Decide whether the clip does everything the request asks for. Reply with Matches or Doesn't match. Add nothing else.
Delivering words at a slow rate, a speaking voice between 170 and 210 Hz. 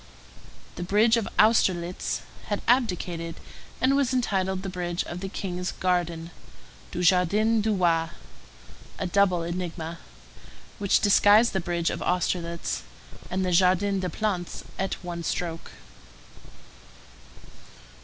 Matches